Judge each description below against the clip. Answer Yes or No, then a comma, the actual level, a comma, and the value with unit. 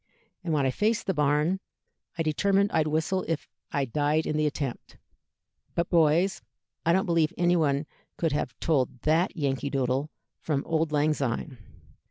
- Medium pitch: Yes, medium, 155 Hz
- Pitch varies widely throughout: No, average, 2.8 semitones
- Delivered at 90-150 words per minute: No, average, 160 wpm